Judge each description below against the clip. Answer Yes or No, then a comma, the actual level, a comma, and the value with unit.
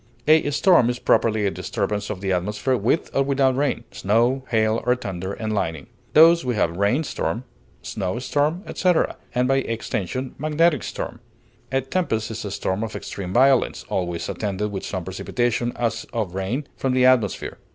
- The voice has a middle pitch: No, low, 115 Hz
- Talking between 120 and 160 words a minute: No, average, 170 wpm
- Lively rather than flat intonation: No, average, 4.7 semitones